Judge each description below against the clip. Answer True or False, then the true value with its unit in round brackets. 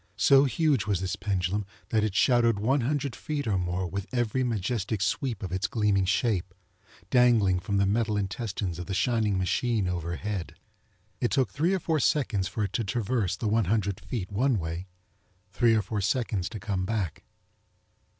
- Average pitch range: True (4.2 semitones)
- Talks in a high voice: False (105 Hz)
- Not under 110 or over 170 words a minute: False (180 wpm)